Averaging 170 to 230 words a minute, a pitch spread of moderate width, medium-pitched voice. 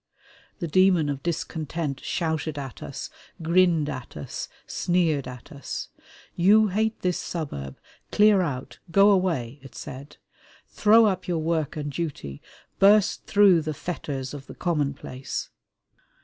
No: slow, 135 wpm; average, 4.7 semitones; medium, 160 Hz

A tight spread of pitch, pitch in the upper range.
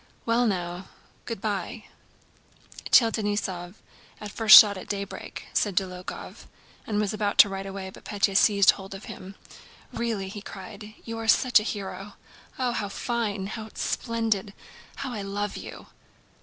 Yes: narrow, 2.3 semitones; high, 205 Hz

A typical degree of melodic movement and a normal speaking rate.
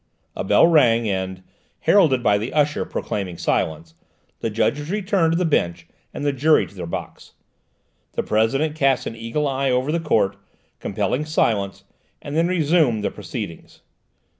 No: wide, 7.2 semitones; average, 160 wpm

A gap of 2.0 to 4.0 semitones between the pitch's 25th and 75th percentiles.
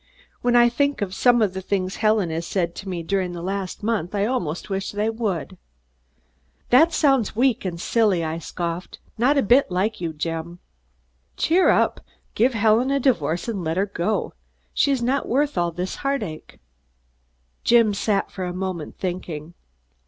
No: average, 5.3 semitones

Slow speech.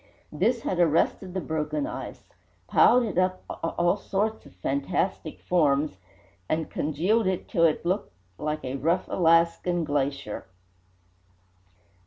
Yes: slow, 130 wpm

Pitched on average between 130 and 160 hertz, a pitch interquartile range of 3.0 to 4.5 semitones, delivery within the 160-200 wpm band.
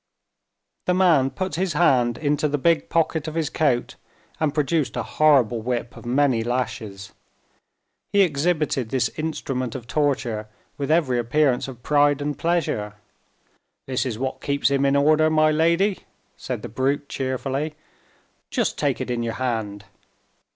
No: medium, 140 Hz; average, 4.1 semitones; average, 150 wpm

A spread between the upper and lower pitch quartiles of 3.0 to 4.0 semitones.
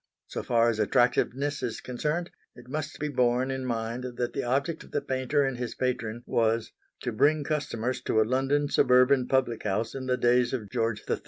No: narrow, 2.5 semitones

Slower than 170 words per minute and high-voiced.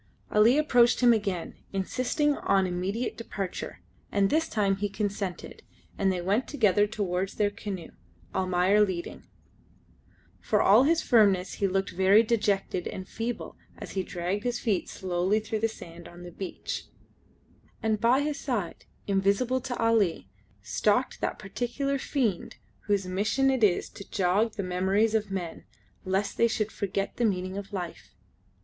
Yes: average, 155 wpm; high, 205 Hz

